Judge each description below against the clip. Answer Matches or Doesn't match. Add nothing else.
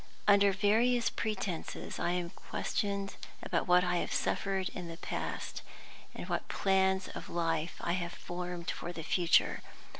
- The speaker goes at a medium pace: Matches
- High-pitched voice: Doesn't match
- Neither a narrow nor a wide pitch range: Doesn't match